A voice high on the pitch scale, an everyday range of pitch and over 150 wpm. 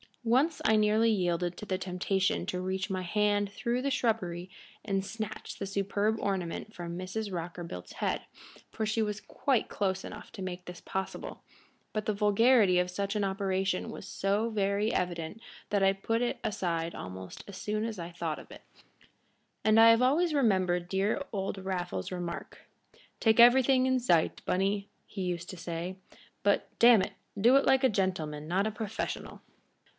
Yes: high, 195 Hz; average, 3.3 semitones; average, 170 wpm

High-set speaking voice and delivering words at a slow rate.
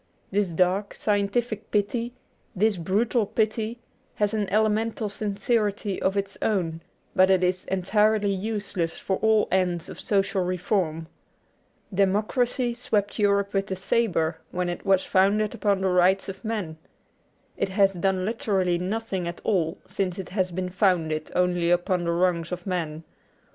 No: high, 195 Hz; average, 150 wpm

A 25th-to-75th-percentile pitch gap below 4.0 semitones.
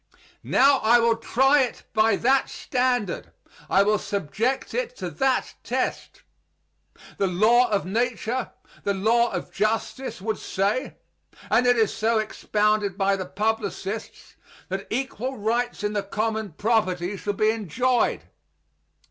Yes: average, 3.4 semitones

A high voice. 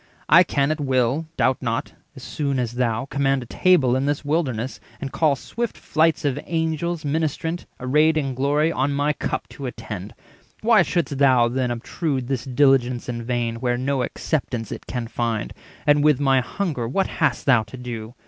No: low, 135 Hz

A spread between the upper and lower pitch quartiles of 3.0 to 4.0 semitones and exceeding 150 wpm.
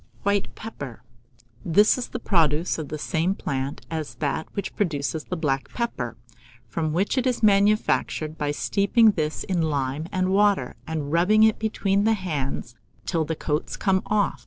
No: average, 5.2 semitones; average, 165 wpm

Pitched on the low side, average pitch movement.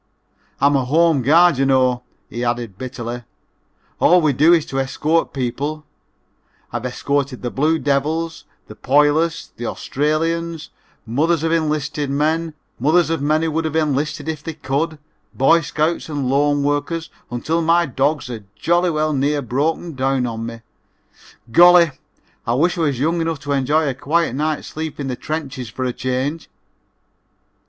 No: medium, 145 Hz; average, 3.5 semitones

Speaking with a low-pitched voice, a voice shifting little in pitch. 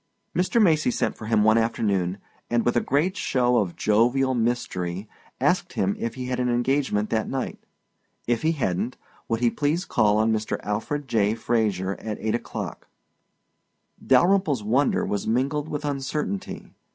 No: low, 120 Hz; average, 4.2 semitones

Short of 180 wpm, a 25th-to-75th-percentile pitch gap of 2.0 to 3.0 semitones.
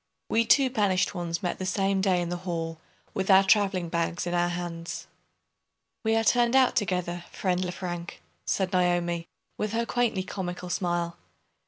Yes: average, 165 wpm; narrow, 2.6 semitones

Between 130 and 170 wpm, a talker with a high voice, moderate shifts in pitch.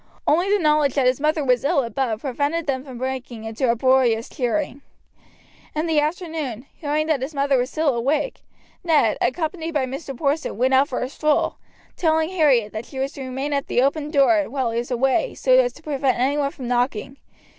No: average, 200 wpm; very high, 275 Hz; average, 3.3 semitones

